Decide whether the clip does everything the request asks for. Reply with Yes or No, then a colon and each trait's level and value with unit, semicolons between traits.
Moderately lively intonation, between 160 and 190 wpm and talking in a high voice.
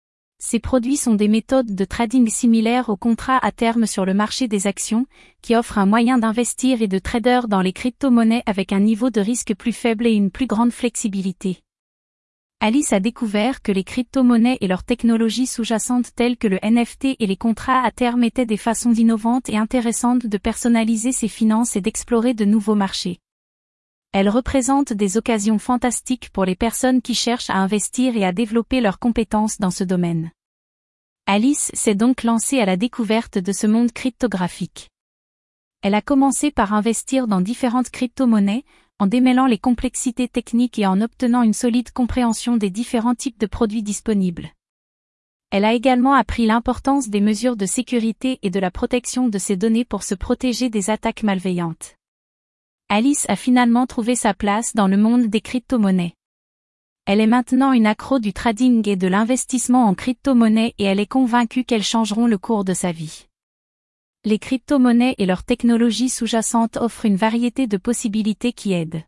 Yes: average, 3.1 semitones; average, 175 wpm; high, 230 Hz